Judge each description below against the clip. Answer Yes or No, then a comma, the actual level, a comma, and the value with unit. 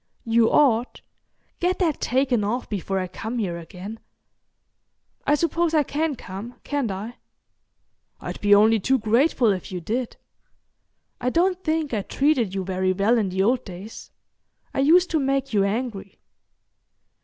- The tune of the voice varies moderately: No, wide, 5.8 semitones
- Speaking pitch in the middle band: No, high, 230 Hz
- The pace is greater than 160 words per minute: No, average, 155 wpm